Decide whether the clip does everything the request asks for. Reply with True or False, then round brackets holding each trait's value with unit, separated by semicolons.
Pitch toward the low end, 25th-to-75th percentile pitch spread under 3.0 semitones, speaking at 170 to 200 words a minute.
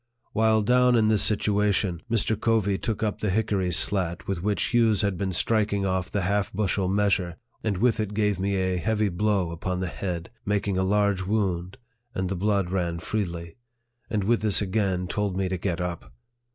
True (100 Hz; 2.6 semitones; 190 wpm)